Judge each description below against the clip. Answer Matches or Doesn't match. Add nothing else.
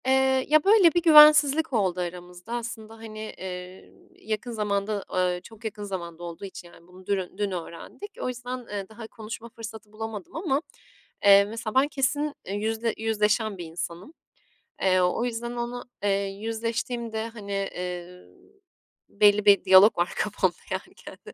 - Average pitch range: Matches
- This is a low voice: Doesn't match